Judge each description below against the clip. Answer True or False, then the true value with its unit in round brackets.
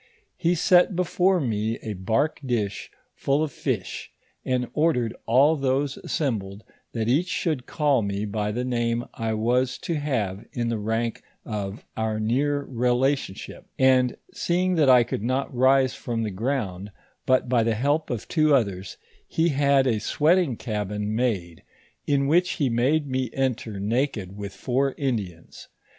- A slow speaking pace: False (155 wpm)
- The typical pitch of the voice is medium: False (125 Hz)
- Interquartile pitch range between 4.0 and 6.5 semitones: True (4.5 semitones)